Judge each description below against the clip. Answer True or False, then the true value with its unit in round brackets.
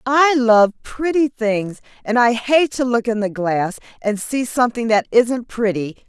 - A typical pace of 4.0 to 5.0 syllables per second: True (4.2 syllables/s)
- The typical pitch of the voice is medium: False (235 Hz)